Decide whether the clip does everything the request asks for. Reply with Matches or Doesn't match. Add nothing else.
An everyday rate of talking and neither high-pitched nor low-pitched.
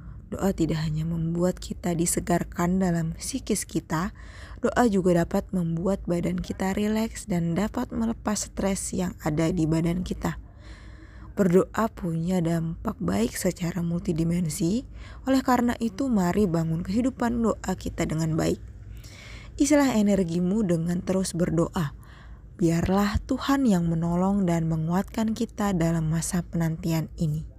Matches